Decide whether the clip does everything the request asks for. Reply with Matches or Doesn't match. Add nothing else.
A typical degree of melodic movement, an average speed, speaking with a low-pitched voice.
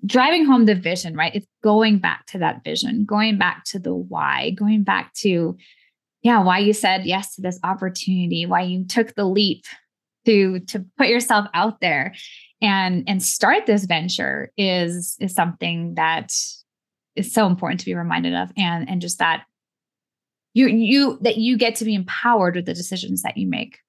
Doesn't match